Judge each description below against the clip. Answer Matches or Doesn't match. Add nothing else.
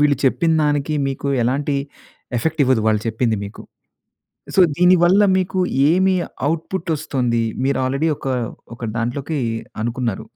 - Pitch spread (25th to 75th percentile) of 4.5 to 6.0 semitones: Matches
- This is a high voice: Doesn't match